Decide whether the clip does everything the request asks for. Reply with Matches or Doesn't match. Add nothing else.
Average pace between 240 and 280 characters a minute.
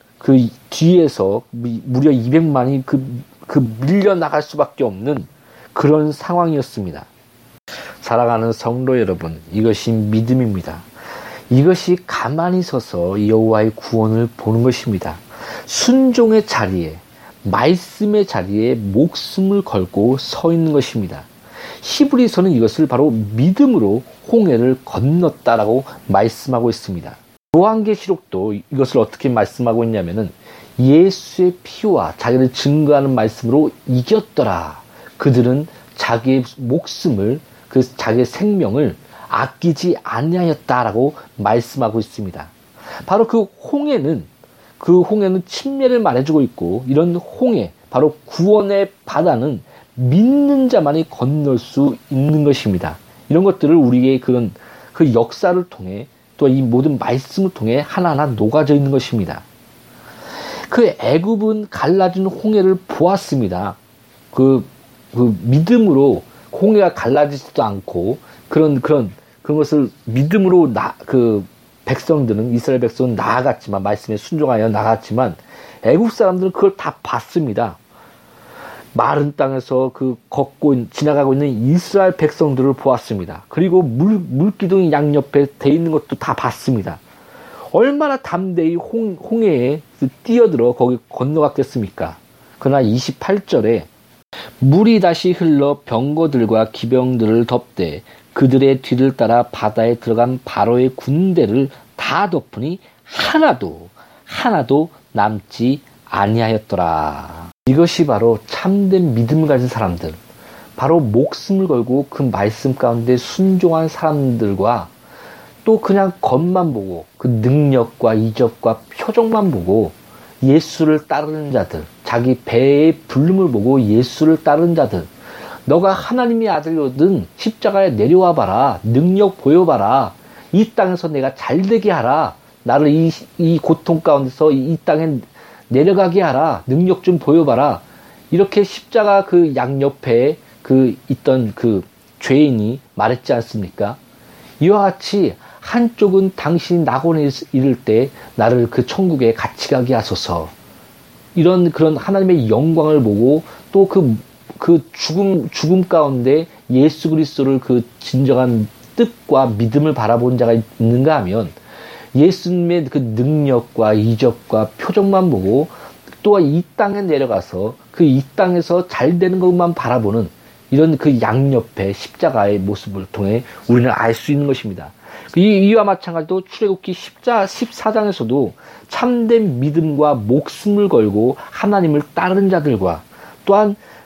Matches